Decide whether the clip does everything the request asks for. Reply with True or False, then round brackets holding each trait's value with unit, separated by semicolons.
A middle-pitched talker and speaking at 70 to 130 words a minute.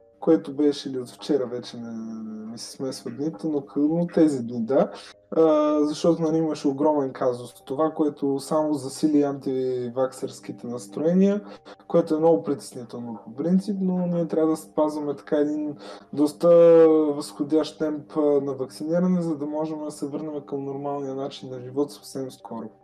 False (145 Hz; 150 wpm)